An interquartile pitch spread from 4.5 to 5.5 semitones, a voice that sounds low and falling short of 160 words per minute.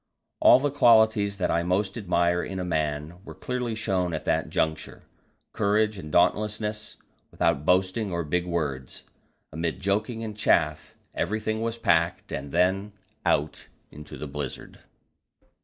Yes: average, 4.8 semitones; very low, 95 Hz; average, 140 wpm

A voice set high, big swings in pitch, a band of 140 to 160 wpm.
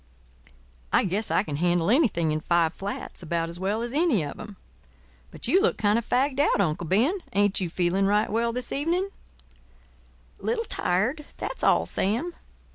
No: high, 210 Hz; wide, 7.3 semitones; average, 170 wpm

